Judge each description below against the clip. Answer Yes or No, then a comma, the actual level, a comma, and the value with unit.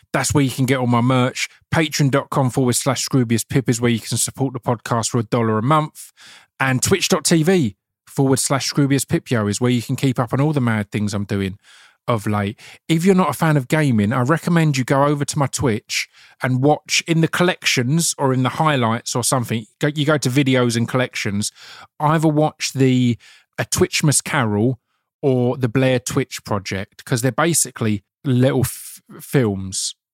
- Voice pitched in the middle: No, low, 130 Hz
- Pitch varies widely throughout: No, average, 3.7 semitones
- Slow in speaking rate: No, average, 185 wpm